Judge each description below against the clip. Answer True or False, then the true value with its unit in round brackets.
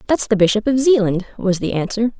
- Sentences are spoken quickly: True (220 wpm)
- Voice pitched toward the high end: True (215 Hz)